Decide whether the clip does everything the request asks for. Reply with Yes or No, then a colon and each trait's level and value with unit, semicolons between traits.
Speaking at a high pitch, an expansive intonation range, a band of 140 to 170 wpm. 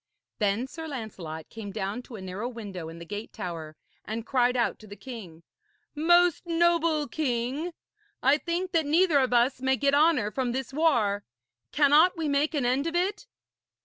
No: very high, 260 Hz; wide, 6.9 semitones; average, 180 wpm